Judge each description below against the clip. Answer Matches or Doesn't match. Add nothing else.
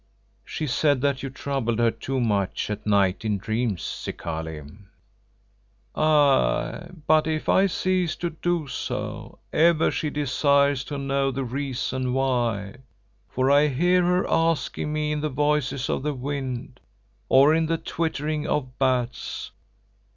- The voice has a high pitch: Doesn't match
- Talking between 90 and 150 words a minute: Matches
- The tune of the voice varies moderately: Matches